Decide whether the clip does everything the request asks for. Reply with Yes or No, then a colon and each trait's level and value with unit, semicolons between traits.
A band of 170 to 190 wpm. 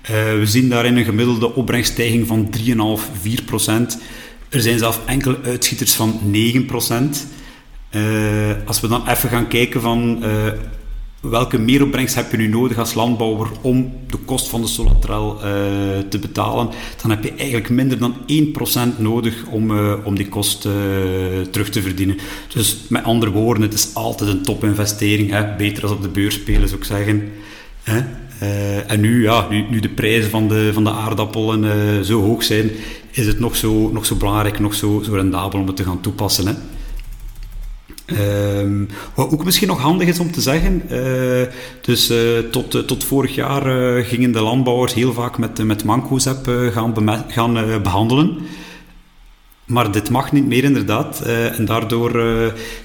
Yes: average, 180 wpm